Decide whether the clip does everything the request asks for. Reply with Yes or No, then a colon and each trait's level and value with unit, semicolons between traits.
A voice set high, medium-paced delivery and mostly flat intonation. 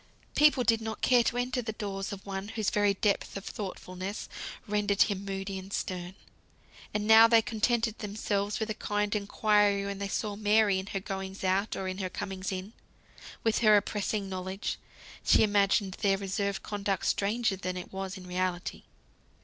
Yes: high, 200 Hz; average, 175 wpm; narrow, 1.8 semitones